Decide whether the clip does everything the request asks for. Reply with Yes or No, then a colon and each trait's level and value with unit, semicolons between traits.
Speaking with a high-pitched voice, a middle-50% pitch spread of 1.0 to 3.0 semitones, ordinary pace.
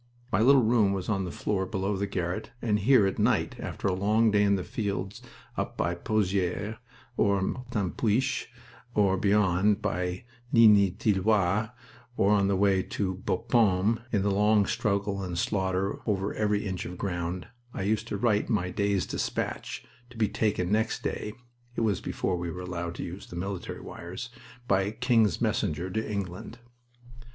No: low, 100 Hz; narrow, 2.5 semitones; average, 165 wpm